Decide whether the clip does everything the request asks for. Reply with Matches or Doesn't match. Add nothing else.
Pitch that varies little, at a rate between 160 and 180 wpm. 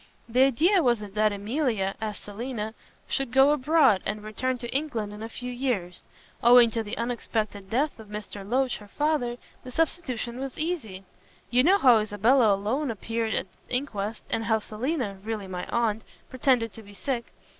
Doesn't match